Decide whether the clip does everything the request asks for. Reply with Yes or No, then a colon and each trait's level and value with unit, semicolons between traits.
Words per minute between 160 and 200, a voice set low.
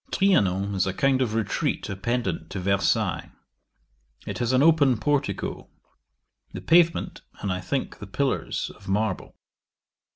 No: slow, 135 wpm; low, 110 Hz